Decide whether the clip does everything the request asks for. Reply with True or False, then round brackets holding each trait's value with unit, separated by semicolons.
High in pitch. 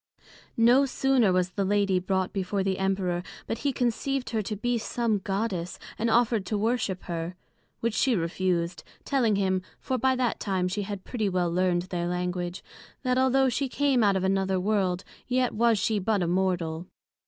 True (200 Hz)